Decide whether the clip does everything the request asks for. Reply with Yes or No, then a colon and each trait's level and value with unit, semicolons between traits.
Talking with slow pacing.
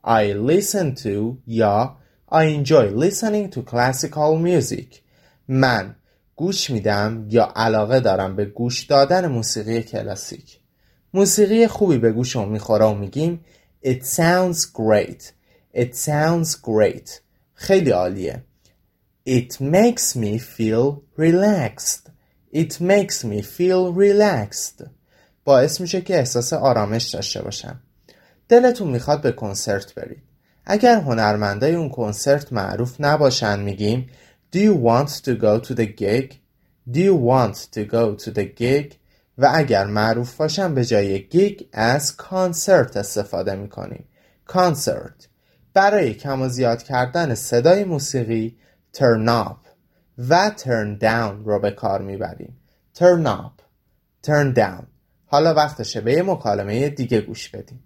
No: average, 125 wpm